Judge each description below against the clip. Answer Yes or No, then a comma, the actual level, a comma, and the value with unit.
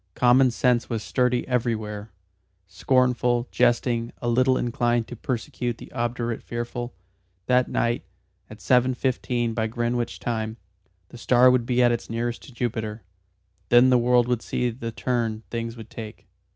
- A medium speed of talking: Yes, average, 150 wpm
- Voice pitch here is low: Yes, low, 120 Hz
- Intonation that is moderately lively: No, narrow, 1.3 semitones